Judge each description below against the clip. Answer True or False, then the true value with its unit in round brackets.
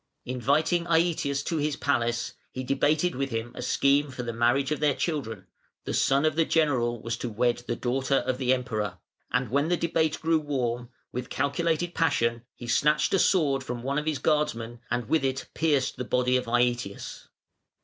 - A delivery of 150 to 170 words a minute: False (190 wpm)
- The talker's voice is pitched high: False (135 Hz)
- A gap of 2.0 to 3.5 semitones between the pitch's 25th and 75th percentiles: False (4.0 semitones)